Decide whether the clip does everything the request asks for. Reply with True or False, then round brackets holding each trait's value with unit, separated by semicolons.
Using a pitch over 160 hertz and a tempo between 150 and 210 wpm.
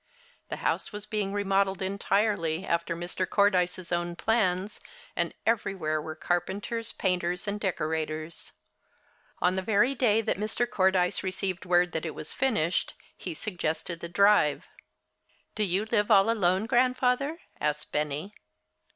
False (190 Hz; 135 wpm)